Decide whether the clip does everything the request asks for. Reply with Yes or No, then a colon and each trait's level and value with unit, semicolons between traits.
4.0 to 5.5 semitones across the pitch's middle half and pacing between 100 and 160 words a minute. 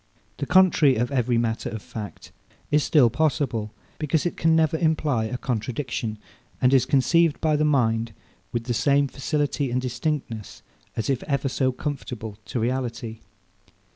Yes: average, 4.3 semitones; average, 155 wpm